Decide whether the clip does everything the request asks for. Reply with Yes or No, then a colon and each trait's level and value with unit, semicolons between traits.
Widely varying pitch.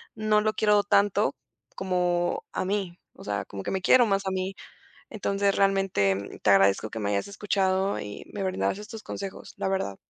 Yes: wide, 7.5 semitones